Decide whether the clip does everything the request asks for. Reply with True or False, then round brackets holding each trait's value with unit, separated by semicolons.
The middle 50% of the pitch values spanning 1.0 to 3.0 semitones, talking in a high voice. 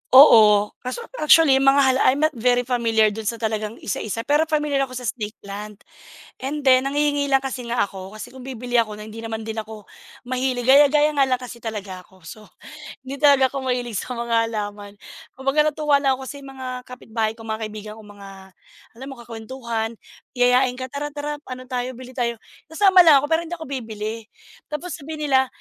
False (3.8 semitones; 250 Hz)